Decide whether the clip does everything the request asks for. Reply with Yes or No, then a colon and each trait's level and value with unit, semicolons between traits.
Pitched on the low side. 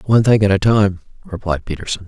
Yes: low, 100 Hz